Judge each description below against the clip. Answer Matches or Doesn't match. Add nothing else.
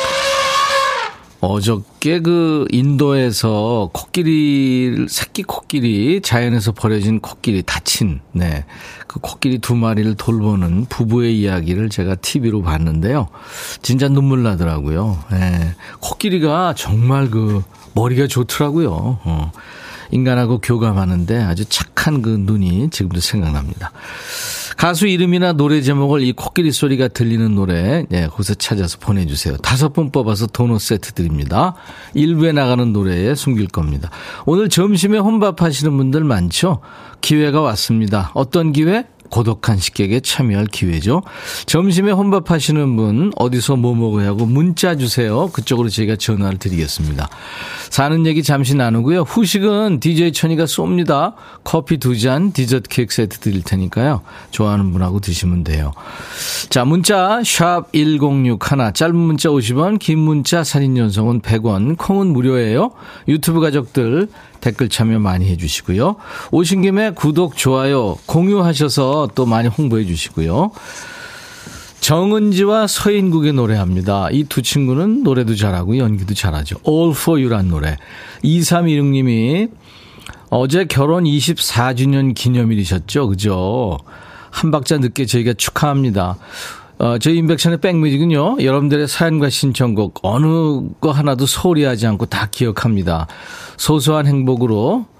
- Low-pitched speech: Matches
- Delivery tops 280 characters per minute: Matches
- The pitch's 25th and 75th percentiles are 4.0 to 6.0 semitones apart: Doesn't match